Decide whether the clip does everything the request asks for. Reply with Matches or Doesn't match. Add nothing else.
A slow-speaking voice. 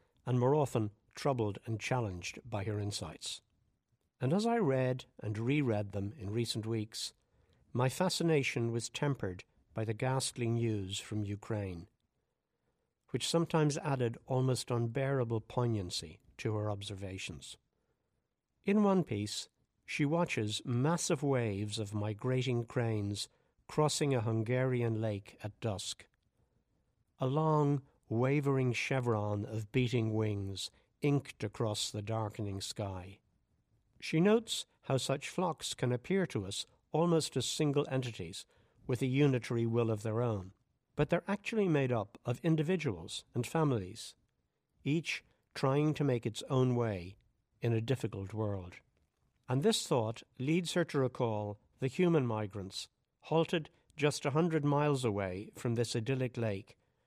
Matches